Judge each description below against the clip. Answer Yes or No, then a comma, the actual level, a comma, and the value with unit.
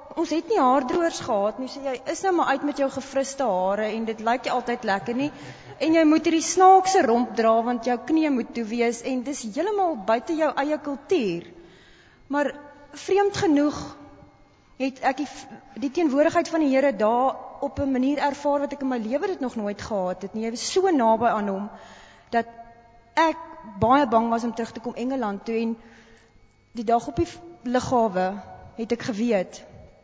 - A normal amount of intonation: Yes, average, 4.5 semitones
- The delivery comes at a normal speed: Yes, average, 190 wpm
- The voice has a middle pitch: No, very high, 260 Hz